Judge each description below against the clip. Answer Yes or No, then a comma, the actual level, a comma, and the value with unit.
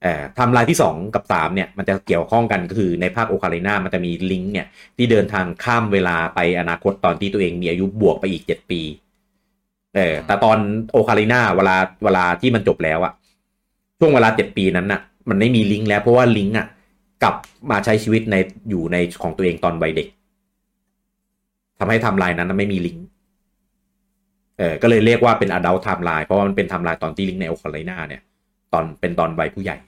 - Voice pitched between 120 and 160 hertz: No, low, 100 Hz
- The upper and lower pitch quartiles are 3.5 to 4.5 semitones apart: No, average, 5.2 semitones